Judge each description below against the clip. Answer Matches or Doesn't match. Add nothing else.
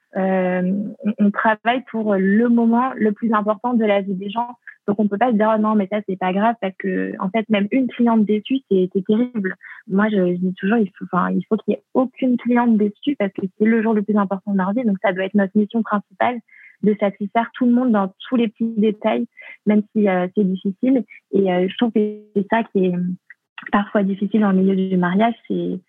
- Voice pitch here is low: Doesn't match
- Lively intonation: Doesn't match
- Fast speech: Matches